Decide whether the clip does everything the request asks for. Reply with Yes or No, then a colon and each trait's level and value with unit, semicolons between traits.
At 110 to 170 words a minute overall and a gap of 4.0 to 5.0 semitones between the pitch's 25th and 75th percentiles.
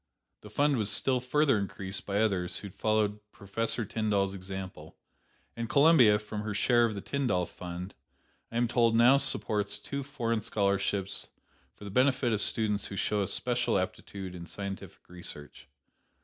No: average, 160 wpm; average, 3.5 semitones